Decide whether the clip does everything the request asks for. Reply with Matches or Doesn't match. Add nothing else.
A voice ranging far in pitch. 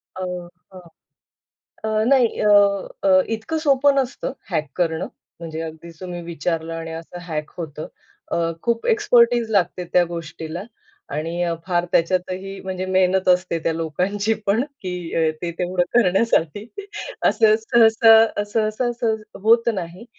Doesn't match